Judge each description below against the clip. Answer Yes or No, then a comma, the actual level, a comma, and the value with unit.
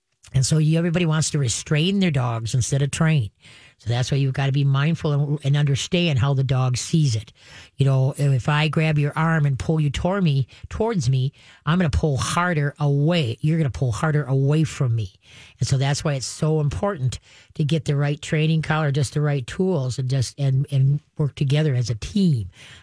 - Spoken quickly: Yes, fast, 215 wpm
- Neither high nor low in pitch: Yes, medium, 145 Hz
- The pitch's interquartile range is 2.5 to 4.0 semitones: Yes, average, 3.0 semitones